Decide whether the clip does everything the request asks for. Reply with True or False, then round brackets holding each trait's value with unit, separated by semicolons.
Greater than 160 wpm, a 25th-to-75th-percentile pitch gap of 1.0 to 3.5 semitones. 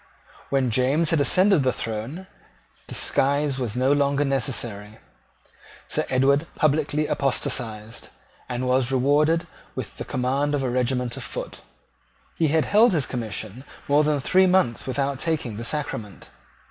False (140 wpm; 3.2 semitones)